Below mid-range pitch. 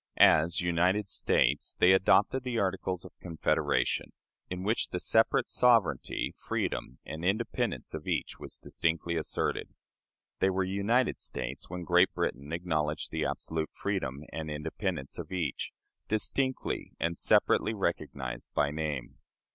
Yes: very low, 85 Hz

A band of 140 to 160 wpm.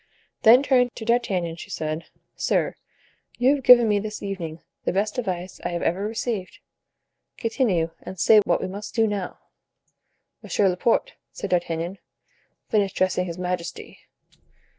Yes: average, 145 wpm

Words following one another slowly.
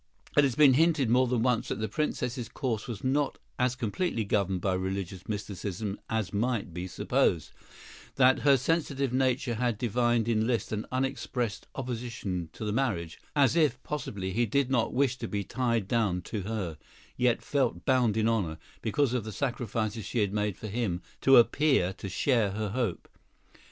No: average, 175 wpm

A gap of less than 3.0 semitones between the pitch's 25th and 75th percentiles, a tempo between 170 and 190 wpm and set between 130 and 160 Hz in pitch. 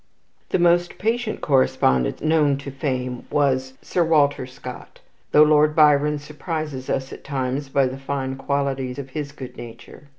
No: narrow, 2.4 semitones; average, 155 wpm; medium, 140 Hz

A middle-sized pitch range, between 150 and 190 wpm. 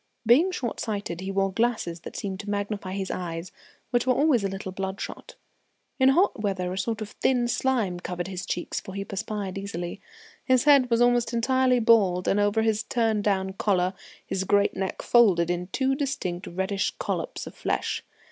Yes: average, 4.0 semitones; average, 185 wpm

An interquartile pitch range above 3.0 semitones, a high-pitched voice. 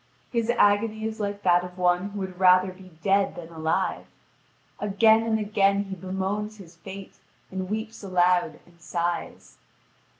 No: narrow, 2.5 semitones; high, 195 Hz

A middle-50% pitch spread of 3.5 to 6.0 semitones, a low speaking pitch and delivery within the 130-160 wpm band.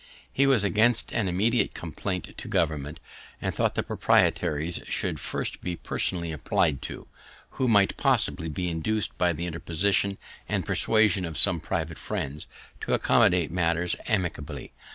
Yes: average, 4.0 semitones; very low, 90 Hz; average, 145 wpm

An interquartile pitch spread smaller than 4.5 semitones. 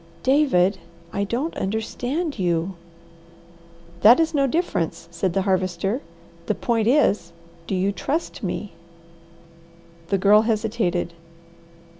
No: average, 5.3 semitones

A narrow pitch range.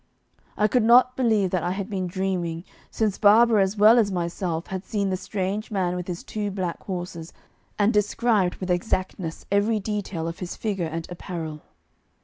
No: average, 3.0 semitones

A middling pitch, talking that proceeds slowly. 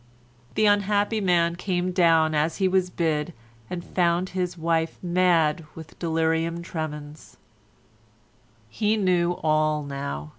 Yes: medium, 170 Hz; slow, 120 wpm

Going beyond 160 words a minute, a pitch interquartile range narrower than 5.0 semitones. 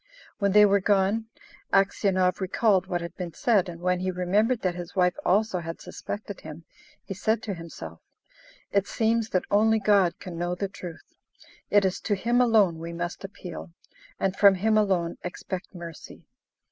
Yes: average, 170 wpm; average, 2.8 semitones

